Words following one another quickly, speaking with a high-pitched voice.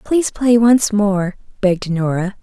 No: average, 150 wpm; high, 205 Hz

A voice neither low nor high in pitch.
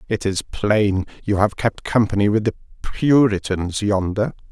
No: low, 105 Hz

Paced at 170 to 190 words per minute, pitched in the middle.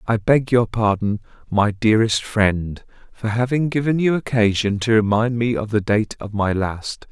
No: average, 175 wpm; low, 110 Hz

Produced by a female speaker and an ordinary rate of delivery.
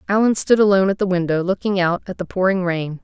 No: female; fast, 235 wpm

